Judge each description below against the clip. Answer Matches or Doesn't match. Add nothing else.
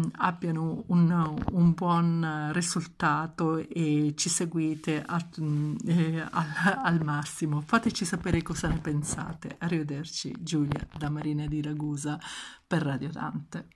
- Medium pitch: Matches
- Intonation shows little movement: Matches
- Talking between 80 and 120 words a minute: Matches